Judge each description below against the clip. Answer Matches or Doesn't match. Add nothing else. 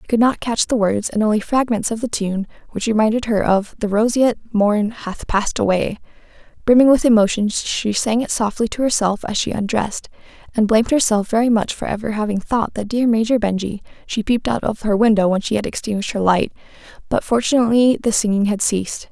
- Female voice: Matches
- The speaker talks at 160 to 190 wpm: Doesn't match